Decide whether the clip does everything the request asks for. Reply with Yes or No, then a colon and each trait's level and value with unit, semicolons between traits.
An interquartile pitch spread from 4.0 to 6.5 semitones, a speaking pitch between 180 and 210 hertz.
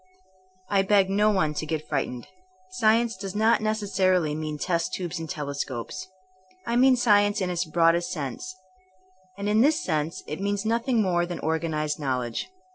Yes: average, 5.2 semitones; medium, 185 Hz